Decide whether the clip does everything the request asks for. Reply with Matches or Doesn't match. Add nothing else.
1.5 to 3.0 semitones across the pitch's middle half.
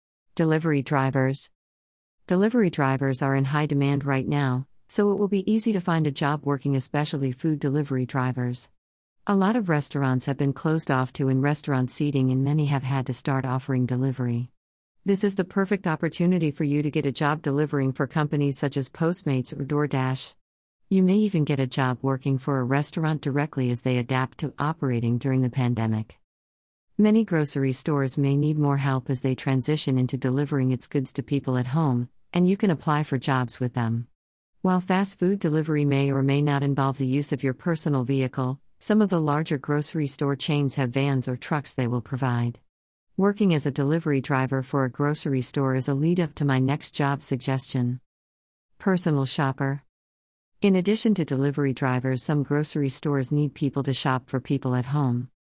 Matches